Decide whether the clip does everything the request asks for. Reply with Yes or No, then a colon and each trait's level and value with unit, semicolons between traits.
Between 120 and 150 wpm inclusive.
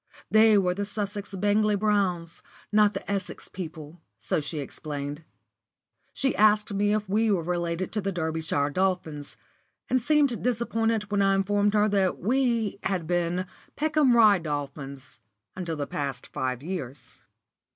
Yes: average, 145 wpm